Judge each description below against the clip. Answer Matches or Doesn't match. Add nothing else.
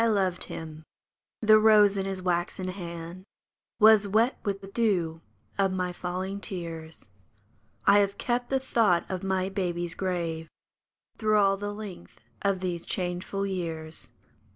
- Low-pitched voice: Doesn't match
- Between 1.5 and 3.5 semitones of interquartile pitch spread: Matches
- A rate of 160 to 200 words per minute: Doesn't match